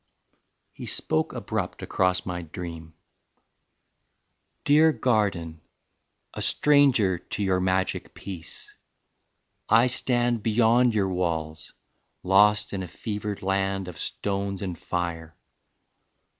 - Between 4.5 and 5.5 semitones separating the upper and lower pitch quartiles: No, average, 3.7 semitones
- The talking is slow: Yes, slow, 105 wpm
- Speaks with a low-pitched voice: Yes, very low, 95 Hz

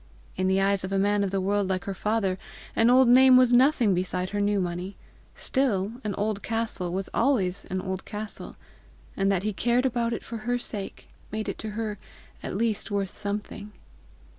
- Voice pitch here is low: No, high, 205 Hz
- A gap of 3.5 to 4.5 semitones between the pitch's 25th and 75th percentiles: No, average, 2.9 semitones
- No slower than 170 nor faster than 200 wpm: Yes, average, 190 wpm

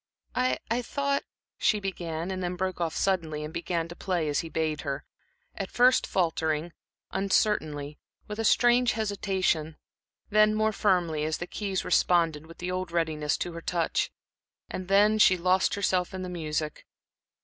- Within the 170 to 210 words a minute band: No, average, 160 wpm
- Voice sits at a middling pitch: Yes, medium, 180 Hz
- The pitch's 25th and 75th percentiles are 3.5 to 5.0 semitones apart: Yes, average, 3.9 semitones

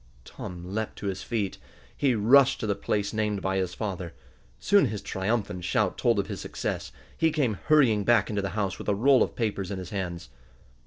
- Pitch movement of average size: Yes, average, 3.4 semitones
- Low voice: Yes, low, 105 Hz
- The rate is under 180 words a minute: No, fast, 205 wpm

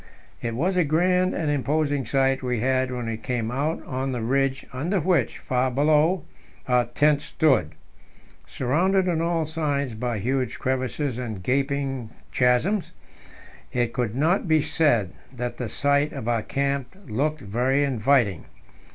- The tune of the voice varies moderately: Yes, average, 3.8 semitones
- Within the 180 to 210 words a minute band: No, average, 150 wpm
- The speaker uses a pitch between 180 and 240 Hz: No, low, 135 Hz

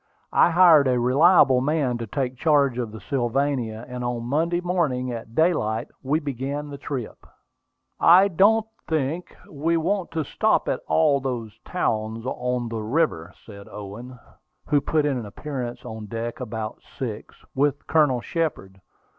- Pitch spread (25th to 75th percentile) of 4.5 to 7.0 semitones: Yes, average, 4.8 semitones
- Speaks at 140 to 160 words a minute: Yes, average, 155 wpm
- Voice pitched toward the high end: No, low, 130 Hz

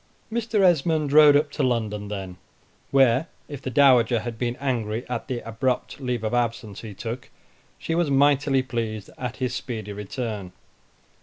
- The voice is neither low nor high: No, low, 125 Hz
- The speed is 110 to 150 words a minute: No, average, 160 wpm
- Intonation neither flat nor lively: Yes, average, 3.9 semitones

